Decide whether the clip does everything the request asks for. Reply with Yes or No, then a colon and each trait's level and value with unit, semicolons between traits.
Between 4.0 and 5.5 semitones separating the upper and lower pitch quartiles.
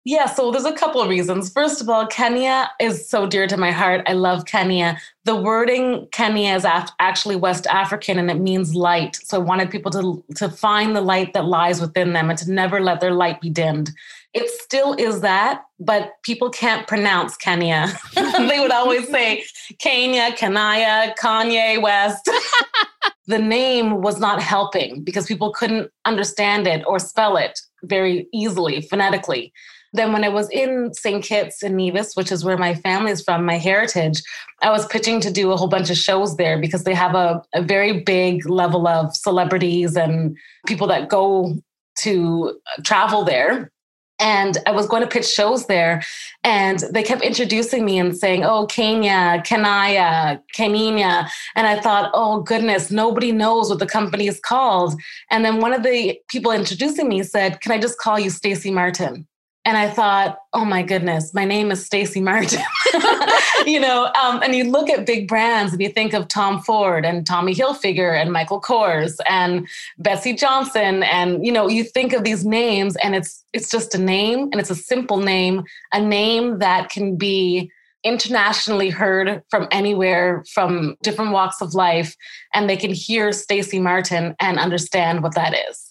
No: average, 3.4 semitones